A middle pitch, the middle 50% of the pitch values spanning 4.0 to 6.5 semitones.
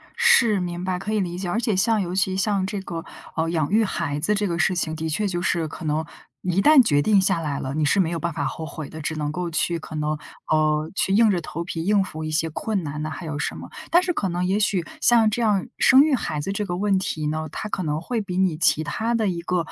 Yes: medium, 175 Hz; average, 4.5 semitones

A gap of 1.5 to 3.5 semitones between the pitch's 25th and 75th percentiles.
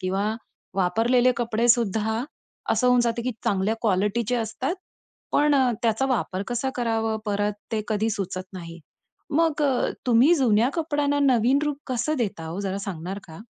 No: average, 4.0 semitones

